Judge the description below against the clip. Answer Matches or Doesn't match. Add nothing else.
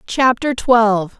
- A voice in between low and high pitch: Doesn't match